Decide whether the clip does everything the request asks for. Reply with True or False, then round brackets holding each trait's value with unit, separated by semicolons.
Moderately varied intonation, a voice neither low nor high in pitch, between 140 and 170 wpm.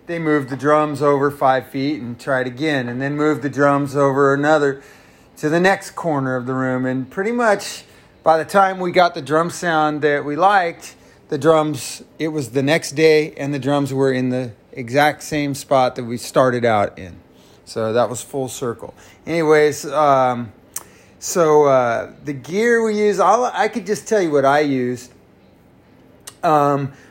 False (3.3 semitones; 145 Hz; 180 wpm)